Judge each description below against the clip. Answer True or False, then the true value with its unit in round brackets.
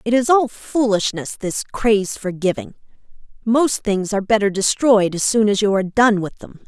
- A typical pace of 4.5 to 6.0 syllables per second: True (5.0 syllables/s)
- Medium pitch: False (215 Hz)